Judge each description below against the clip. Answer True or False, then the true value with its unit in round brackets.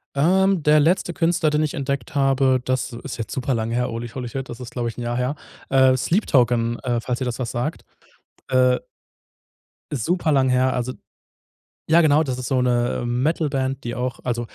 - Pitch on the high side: False (130 Hz)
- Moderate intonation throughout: True (3.0 semitones)